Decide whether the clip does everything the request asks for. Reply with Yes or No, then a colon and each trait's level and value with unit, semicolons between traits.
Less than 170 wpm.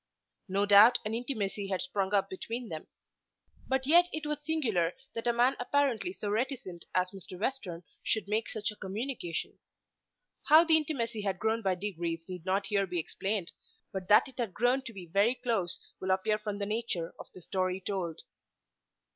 No: average, 180 wpm